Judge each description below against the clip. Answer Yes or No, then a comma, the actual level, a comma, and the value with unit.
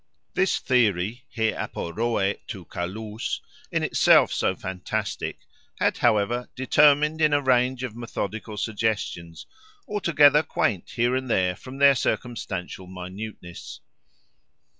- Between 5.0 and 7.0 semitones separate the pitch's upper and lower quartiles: Yes, wide, 5.4 semitones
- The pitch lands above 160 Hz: No, low, 115 Hz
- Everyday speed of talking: No, slow, 95 wpm